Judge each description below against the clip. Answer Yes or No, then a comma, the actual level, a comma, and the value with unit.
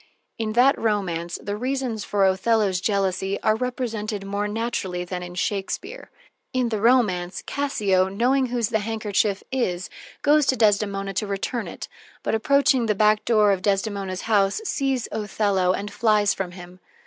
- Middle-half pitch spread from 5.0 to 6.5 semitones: No, average, 3.3 semitones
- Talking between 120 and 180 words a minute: Yes, average, 155 wpm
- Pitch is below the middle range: No, high, 210 Hz